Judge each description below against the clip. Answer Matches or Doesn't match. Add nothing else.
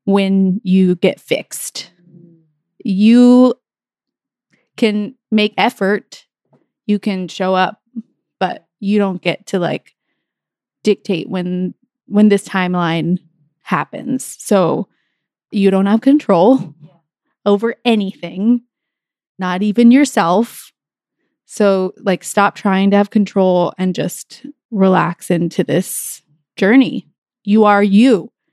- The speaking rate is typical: Doesn't match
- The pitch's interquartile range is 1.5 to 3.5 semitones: Doesn't match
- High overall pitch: Matches